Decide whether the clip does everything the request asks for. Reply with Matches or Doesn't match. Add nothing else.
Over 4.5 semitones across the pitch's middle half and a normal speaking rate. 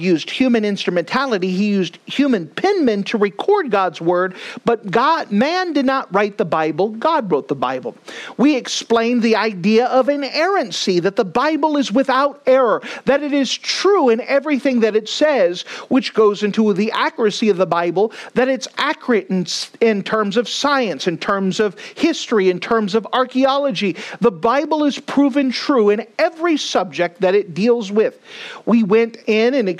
Matches